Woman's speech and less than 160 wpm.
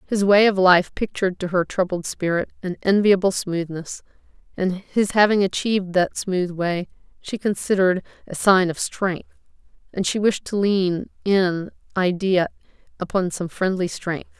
Yes: female; average, 150 wpm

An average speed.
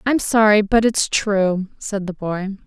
Yes: average, 180 wpm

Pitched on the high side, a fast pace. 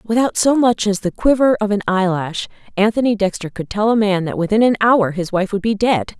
Yes: high, 205 Hz; fast, 230 wpm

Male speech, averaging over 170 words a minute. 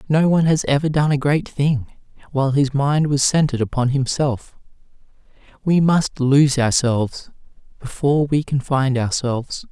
No: male; average, 150 wpm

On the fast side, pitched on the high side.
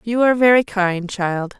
No: average, 190 wpm; high, 210 Hz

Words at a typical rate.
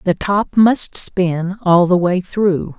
Yes: average, 170 wpm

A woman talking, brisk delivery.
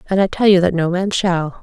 Yes: female; fast, 295 wpm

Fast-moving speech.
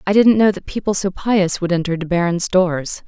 Yes: fast, 235 wpm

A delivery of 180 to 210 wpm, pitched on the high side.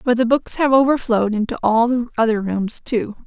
Yes: average, 200 wpm; high, 235 Hz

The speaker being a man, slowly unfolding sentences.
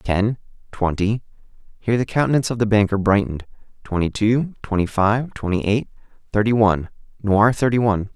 Yes: male; slow, 110 wpm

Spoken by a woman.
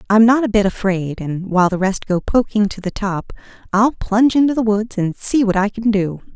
Yes: female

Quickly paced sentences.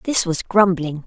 No: average, 170 wpm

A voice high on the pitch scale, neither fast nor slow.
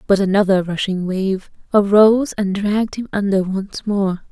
Yes: high, 200 Hz; average, 155 wpm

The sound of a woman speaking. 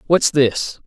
No: male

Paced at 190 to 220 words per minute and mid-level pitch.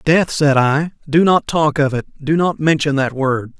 Yes: average, 200 wpm; medium, 150 Hz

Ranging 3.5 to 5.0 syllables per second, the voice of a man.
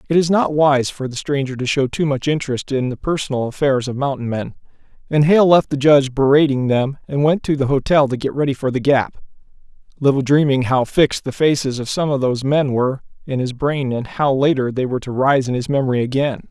No: 5.9 syllables/s; male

